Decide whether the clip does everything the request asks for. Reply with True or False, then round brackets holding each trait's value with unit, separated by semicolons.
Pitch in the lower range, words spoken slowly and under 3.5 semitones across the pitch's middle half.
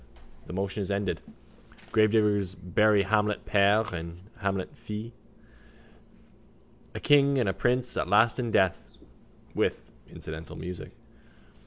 True (100 Hz; 120 wpm; 2.6 semitones)